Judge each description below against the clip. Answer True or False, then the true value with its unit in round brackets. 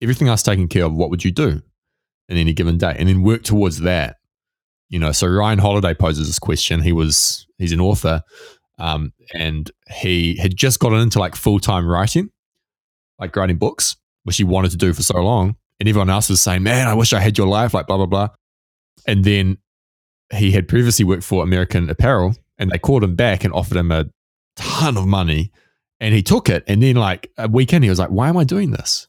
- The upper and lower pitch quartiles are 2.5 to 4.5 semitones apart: True (4.0 semitones)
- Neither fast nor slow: False (220 wpm)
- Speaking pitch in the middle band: False (95 Hz)